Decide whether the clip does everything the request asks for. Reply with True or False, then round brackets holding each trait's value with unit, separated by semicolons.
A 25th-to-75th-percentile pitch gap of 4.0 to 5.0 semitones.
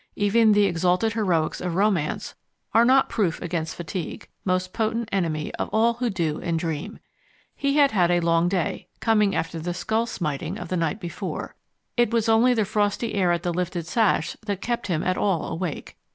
True (4.5 semitones)